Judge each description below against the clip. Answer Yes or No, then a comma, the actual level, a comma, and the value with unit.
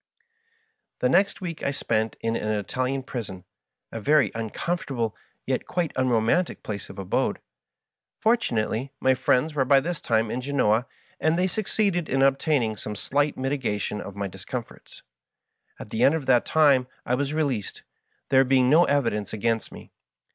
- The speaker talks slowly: No, average, 155 wpm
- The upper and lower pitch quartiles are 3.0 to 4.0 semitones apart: No, average, 4.9 semitones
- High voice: No, low, 130 Hz